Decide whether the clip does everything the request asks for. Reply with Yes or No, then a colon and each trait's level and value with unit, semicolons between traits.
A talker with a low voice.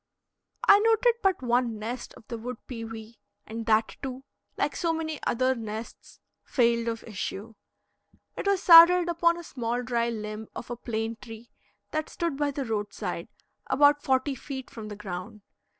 No: high, 240 Hz